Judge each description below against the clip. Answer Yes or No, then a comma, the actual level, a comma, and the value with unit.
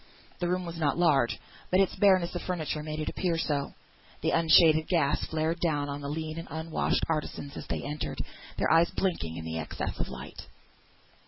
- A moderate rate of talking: Yes, average, 185 wpm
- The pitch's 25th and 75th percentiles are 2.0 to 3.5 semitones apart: Yes, average, 2.8 semitones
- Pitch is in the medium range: Yes, medium, 160 Hz